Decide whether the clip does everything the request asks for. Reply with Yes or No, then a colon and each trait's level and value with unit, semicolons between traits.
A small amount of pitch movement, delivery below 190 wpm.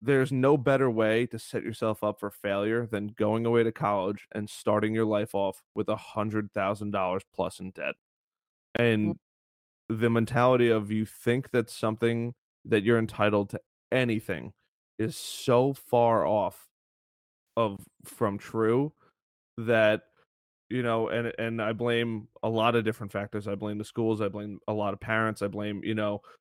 Yes: narrow, 2.0 semitones; average, 170 wpm